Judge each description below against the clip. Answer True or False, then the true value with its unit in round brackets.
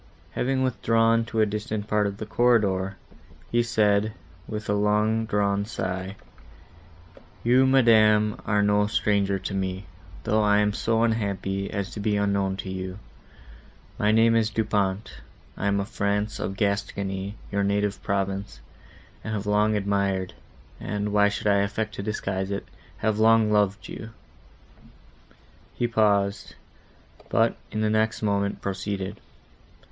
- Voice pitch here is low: True (105 Hz)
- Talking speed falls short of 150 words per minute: True (140 wpm)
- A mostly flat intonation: True (1.6 semitones)